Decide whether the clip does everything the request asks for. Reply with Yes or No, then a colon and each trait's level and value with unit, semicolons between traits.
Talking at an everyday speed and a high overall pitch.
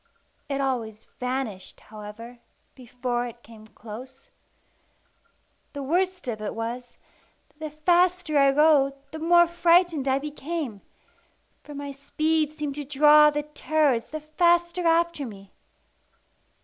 No: slow, 125 wpm; very high, 285 Hz